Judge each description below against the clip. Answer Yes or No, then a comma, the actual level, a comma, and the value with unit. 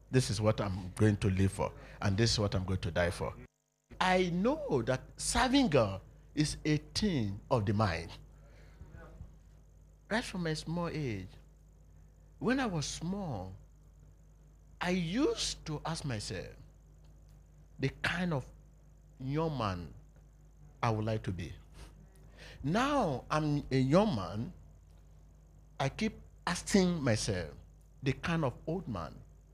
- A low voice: Yes, low, 115 Hz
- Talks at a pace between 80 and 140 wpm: Yes, slow, 135 wpm